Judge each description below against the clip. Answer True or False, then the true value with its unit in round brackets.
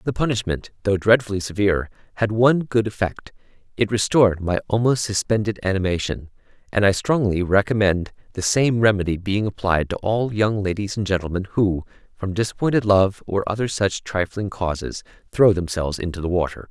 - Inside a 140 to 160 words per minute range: True (155 wpm)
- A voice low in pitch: True (100 Hz)